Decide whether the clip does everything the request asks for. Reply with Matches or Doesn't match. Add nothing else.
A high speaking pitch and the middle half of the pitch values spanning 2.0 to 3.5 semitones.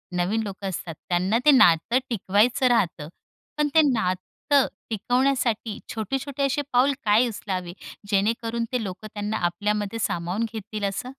Doesn't match